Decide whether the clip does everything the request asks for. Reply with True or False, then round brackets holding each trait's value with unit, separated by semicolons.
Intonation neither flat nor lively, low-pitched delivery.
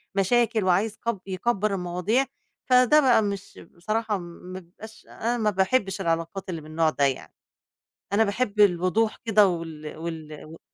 False (4.4 semitones; 195 Hz)